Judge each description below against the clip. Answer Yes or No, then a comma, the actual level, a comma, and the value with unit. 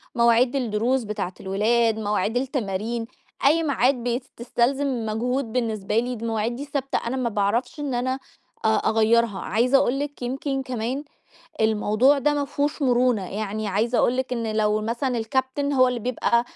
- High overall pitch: Yes, high, 240 Hz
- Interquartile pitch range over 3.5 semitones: No, average, 3.2 semitones